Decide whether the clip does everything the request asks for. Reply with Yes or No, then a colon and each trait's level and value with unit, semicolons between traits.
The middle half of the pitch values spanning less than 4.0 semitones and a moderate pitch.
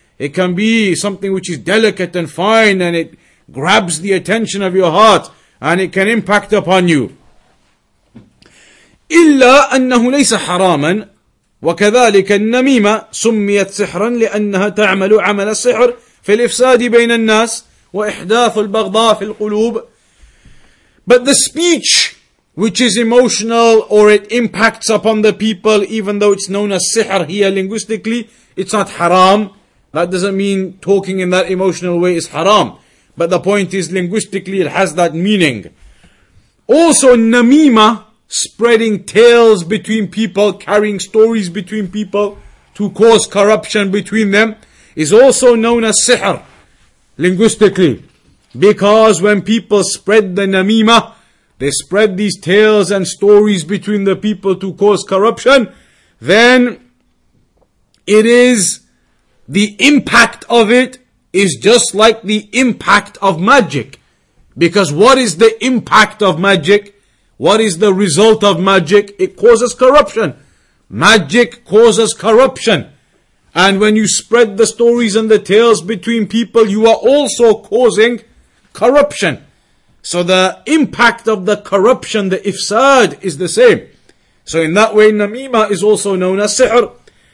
No: average, 2.9 semitones; high, 210 Hz